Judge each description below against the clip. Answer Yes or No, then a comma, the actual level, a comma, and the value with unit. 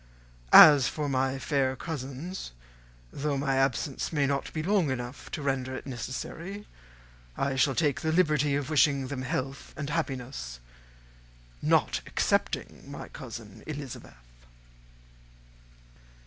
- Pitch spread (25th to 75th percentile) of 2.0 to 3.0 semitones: Yes, narrow, 2.6 semitones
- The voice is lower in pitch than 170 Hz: Yes, medium, 140 Hz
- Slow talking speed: Yes, slow, 125 wpm